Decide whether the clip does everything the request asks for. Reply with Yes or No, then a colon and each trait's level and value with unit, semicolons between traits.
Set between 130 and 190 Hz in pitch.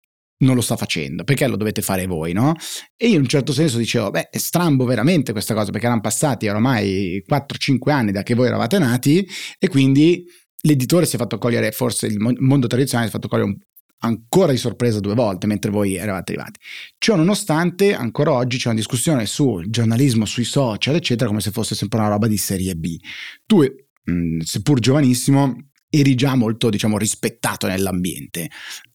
No: low, 120 Hz